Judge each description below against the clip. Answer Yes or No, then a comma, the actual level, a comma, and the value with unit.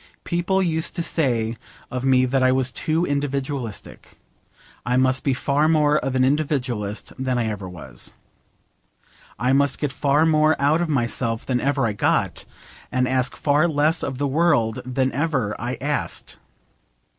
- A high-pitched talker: No, low, 135 Hz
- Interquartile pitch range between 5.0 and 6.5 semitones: No, average, 3.1 semitones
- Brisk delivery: No, average, 160 wpm